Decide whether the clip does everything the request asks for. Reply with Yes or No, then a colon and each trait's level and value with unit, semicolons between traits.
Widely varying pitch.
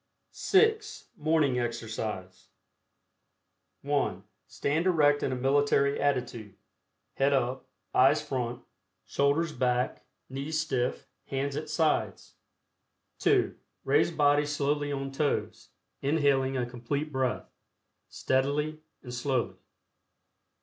No: average, 2.7 semitones